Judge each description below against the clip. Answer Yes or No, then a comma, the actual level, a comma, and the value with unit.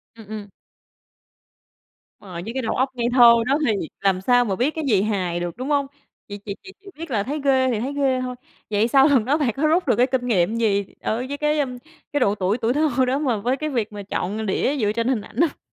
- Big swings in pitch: No, average, 4.8 semitones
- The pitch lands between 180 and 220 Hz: No, high, 245 Hz